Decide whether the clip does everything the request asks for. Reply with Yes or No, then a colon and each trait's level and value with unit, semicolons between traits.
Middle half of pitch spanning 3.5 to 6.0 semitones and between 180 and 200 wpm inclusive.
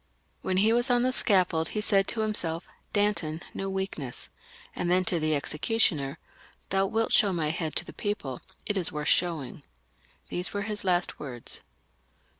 Yes: average, 4.6 semitones; average, 185 wpm